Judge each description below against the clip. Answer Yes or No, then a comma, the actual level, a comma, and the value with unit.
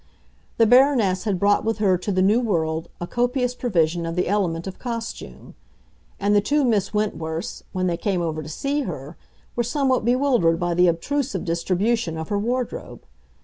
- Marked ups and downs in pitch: Yes, wide, 6.1 semitones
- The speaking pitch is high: Yes, high, 200 Hz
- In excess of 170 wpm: Yes, average, 180 wpm